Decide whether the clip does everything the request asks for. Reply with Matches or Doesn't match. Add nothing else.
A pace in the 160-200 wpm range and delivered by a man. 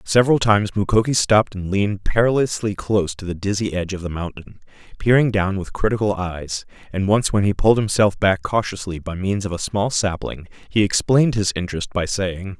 Matches